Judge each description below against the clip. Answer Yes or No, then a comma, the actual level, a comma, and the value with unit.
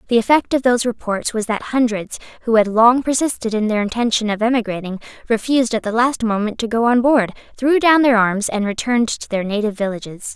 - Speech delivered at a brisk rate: Yes, fast, 210 wpm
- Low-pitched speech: No, high, 230 Hz